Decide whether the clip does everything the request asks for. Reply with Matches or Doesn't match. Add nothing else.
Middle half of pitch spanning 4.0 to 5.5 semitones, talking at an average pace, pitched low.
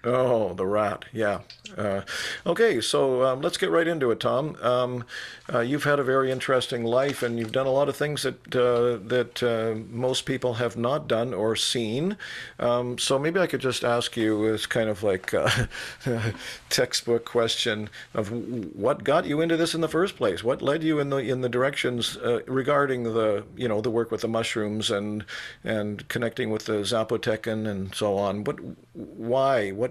Doesn't match